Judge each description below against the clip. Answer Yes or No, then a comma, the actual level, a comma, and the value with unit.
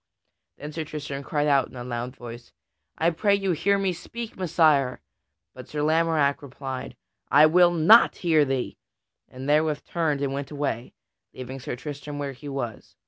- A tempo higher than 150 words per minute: Yes, average, 170 wpm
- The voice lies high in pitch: No, medium, 145 Hz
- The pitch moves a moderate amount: Yes, average, 3.4 semitones